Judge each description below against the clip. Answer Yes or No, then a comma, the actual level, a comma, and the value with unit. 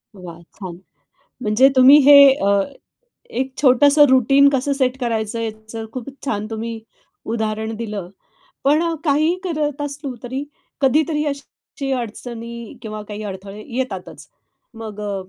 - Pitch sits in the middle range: No, high, 240 Hz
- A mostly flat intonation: No, average, 4.6 semitones